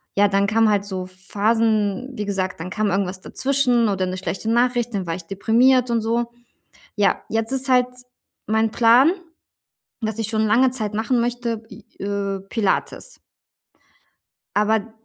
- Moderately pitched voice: No, high, 220 Hz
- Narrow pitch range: No, average, 3.0 semitones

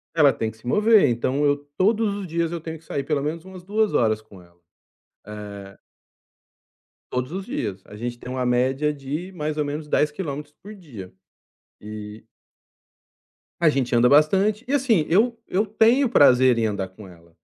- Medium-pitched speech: Yes, medium, 145 Hz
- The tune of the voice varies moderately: No, wide, 8.2 semitones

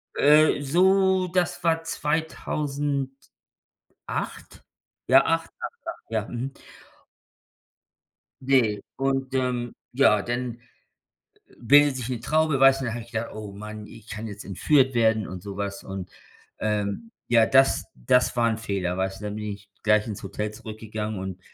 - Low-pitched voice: Yes, low, 115 Hz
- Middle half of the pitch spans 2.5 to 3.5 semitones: No, average, 4.5 semitones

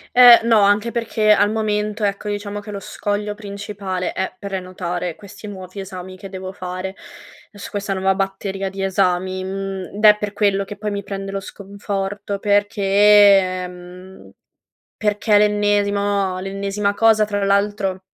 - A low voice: No, high, 200 Hz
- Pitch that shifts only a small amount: Yes, narrow, 1.4 semitones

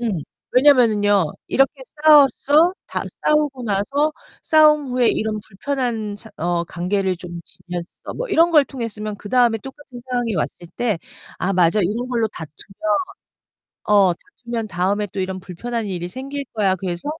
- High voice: Yes, high, 220 Hz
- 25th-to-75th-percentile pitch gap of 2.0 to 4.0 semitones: No, wide, 5.9 semitones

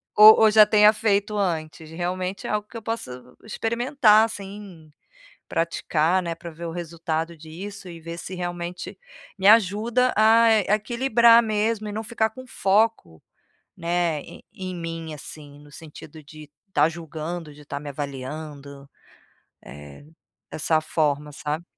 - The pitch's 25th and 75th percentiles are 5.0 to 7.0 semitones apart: Yes, average, 5.3 semitones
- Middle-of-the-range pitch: Yes, medium, 175 Hz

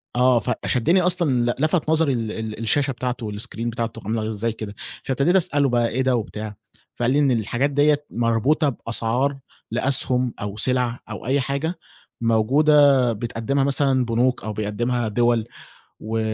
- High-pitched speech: No, low, 125 Hz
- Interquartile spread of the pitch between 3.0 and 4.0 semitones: Yes, average, 3.5 semitones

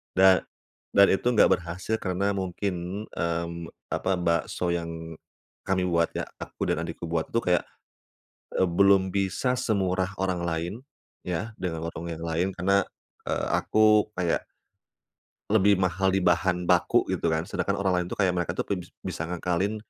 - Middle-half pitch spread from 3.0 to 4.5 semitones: No, narrow, 2.4 semitones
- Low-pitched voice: Yes, very low, 90 Hz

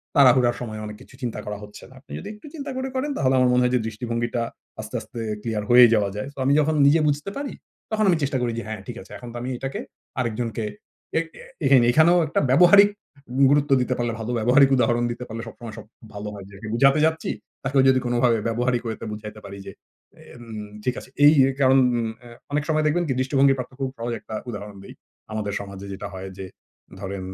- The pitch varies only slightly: No, average, 4.2 semitones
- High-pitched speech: No, low, 125 Hz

